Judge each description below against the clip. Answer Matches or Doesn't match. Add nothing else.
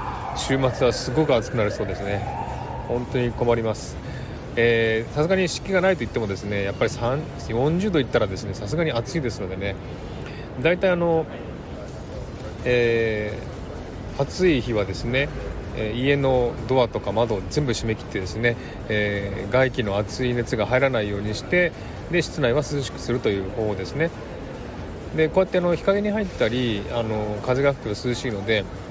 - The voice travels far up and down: Doesn't match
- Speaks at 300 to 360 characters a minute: Matches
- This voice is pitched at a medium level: Doesn't match